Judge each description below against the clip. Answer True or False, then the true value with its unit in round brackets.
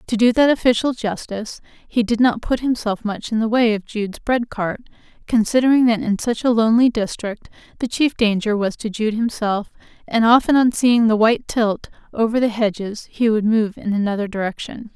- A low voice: False (225 Hz)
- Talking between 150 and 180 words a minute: False (195 wpm)